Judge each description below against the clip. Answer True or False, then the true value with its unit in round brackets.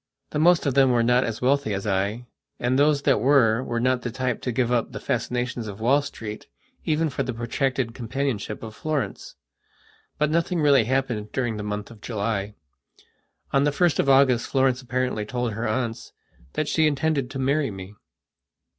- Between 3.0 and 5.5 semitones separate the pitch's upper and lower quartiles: True (3.6 semitones)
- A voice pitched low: True (125 Hz)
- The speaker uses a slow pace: False (185 wpm)